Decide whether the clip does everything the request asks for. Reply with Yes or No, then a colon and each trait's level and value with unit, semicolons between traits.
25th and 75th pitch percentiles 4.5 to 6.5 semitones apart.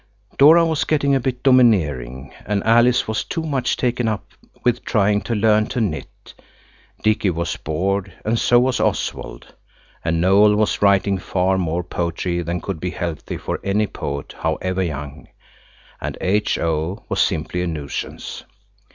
Yes: wide, 5.4 semitones